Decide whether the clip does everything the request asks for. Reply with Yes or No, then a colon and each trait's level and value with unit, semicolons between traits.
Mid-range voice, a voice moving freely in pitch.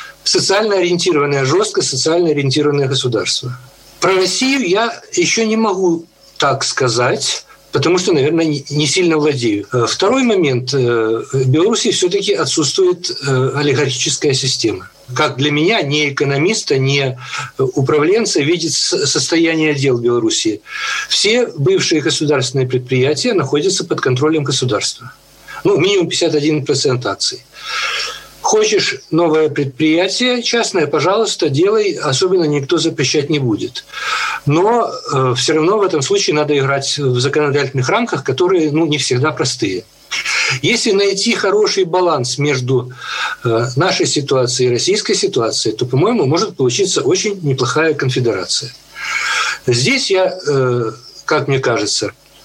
Yes: medium, 155 Hz; wide, 7.5 semitones